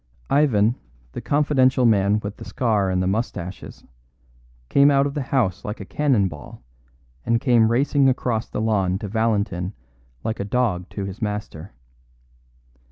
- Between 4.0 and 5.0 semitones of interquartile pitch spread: Yes, average, 4.5 semitones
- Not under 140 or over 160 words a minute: Yes, average, 155 wpm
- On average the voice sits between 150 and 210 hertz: No, low, 110 Hz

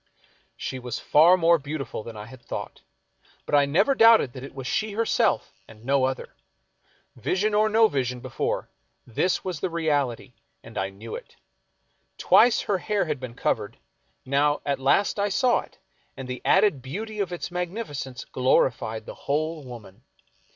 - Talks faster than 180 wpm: No, average, 165 wpm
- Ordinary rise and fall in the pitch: No, wide, 7.1 semitones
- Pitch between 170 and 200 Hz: No, medium, 145 Hz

